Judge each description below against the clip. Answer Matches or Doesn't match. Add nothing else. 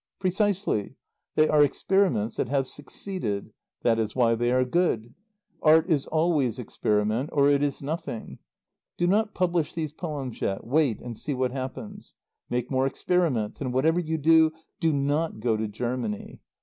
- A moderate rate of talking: Matches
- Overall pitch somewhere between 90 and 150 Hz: Matches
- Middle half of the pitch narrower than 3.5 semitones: Doesn't match